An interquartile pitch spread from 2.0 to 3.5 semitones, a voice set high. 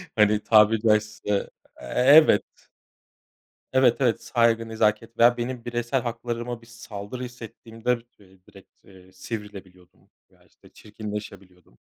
No: narrow, 2.4 semitones; low, 115 Hz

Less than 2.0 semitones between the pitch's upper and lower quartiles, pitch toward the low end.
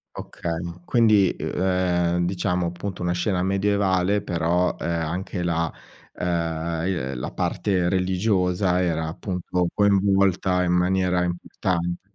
Yes: narrow, 1.5 semitones; very low, 90 Hz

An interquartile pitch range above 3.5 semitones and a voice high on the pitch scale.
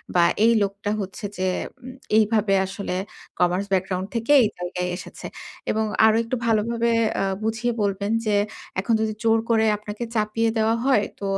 No: narrow, 2.6 semitones; high, 215 Hz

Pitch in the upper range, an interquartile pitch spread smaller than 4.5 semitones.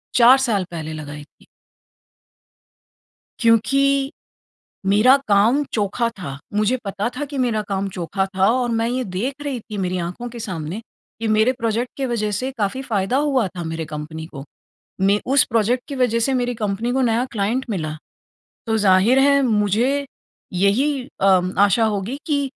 No: high, 220 Hz; average, 4.8 semitones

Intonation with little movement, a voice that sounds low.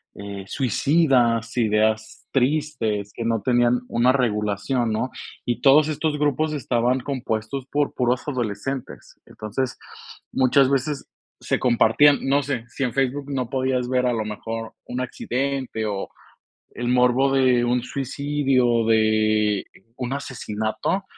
No: average, 3.3 semitones; low, 125 Hz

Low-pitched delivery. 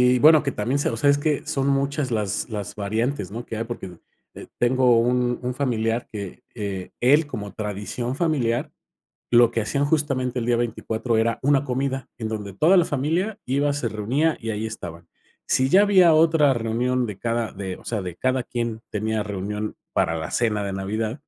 Yes: low, 120 Hz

